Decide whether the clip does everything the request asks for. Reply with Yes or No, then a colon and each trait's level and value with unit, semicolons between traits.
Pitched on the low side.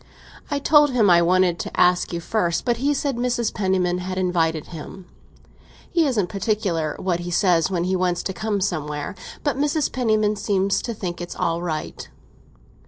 No: medium, 185 Hz